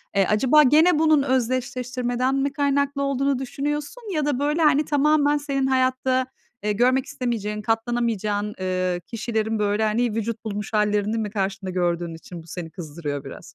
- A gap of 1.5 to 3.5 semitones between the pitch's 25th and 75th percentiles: No, average, 5.0 semitones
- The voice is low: No, high, 240 Hz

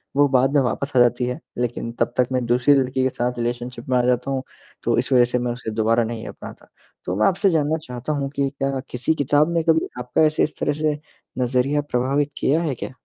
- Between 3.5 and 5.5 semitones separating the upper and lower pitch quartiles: No, average, 2.9 semitones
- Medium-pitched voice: No, low, 130 Hz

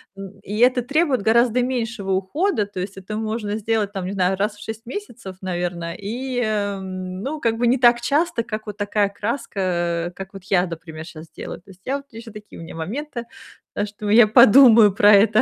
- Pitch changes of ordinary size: Yes, average, 3.8 semitones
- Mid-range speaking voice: No, high, 210 Hz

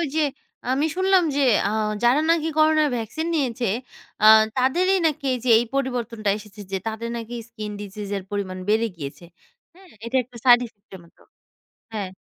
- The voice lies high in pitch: Yes, high, 240 Hz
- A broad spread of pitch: Yes, wide, 6.2 semitones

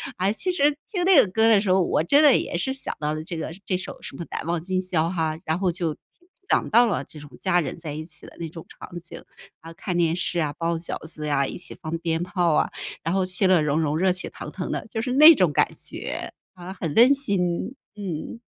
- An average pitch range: Yes, average, 3.6 semitones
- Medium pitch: Yes, medium, 175 Hz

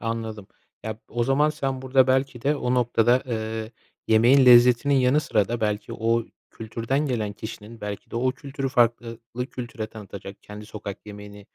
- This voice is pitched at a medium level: No, low, 115 Hz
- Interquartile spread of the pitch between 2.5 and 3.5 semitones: Yes, average, 2.9 semitones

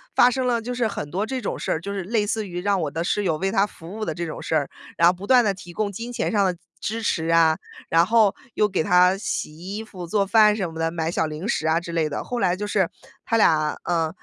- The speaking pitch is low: No, medium, 185 Hz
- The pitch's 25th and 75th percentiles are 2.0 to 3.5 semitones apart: No, average, 4.2 semitones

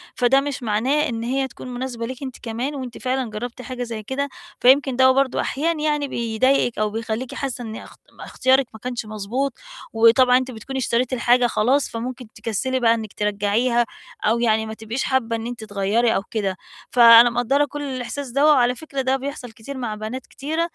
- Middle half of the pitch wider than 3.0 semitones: No, average, 2.7 semitones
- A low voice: No, high, 245 Hz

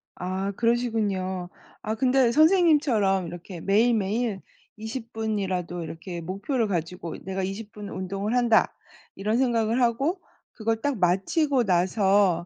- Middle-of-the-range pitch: No, high, 210 Hz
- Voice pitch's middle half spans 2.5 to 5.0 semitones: Yes, average, 4.1 semitones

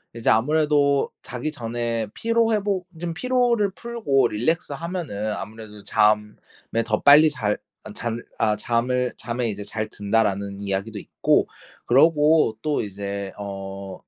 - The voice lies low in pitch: Yes, low, 120 Hz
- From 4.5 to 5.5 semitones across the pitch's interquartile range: No, wide, 6.7 semitones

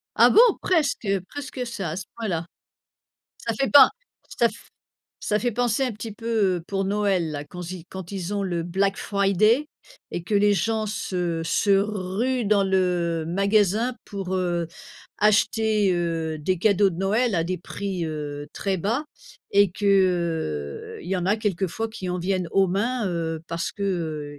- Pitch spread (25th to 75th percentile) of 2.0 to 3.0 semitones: No, average, 3.5 semitones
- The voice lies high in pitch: Yes, high, 195 Hz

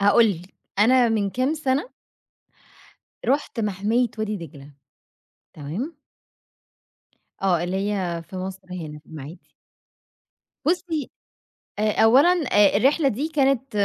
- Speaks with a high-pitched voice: Yes, high, 210 Hz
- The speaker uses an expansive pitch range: Yes, wide, 6.4 semitones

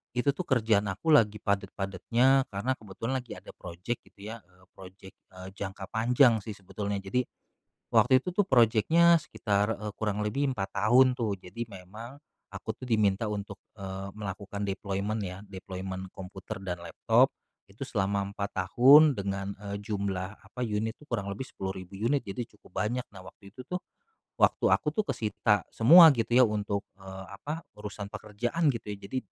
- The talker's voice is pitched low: Yes, low, 105 Hz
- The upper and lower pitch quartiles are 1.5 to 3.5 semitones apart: No, average, 3.9 semitones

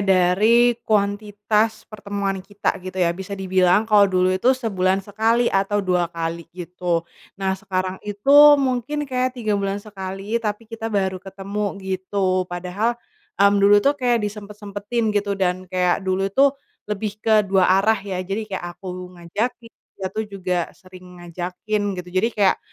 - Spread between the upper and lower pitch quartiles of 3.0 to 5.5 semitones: No, narrow, 2.5 semitones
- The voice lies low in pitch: No, high, 200 Hz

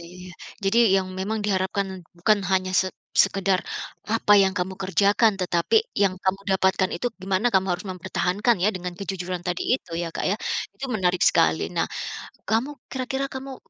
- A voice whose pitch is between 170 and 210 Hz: Yes, high, 190 Hz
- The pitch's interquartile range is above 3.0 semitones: No, narrow, 2.4 semitones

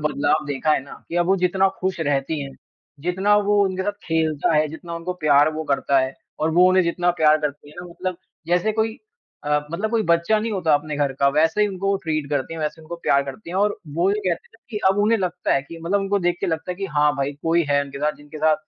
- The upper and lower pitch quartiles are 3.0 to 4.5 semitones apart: Yes, average, 4.1 semitones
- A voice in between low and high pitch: Yes, medium, 165 Hz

